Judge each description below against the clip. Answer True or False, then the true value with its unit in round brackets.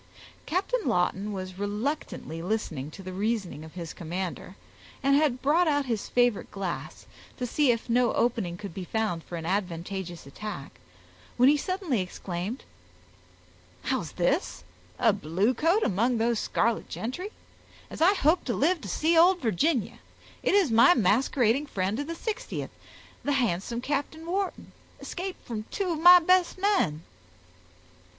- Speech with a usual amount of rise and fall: False (8.5 semitones)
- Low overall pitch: False (235 Hz)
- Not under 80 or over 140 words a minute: False (150 wpm)